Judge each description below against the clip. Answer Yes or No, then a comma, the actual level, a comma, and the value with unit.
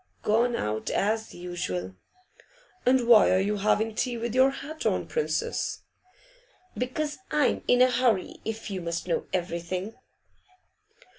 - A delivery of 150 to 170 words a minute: No, slow, 135 wpm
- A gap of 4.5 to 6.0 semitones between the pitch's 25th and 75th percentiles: Yes, wide, 5.5 semitones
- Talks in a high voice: Yes, high, 220 Hz